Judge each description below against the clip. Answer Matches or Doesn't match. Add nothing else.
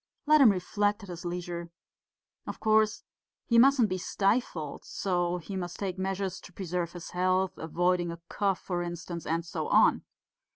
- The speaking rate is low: Doesn't match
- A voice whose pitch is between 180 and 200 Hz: Matches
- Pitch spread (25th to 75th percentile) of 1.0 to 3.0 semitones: Matches